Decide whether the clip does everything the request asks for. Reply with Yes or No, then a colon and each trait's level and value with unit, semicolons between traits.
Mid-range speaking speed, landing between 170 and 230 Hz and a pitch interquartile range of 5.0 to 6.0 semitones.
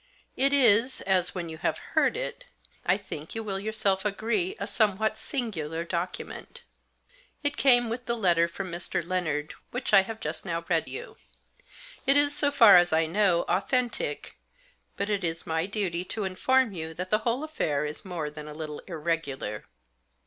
Yes: average, 175 wpm; high, 190 Hz; wide, 5.4 semitones